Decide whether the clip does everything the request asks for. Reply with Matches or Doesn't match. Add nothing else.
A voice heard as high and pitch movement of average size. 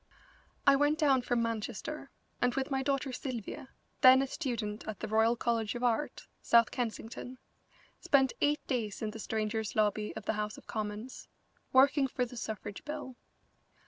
Matches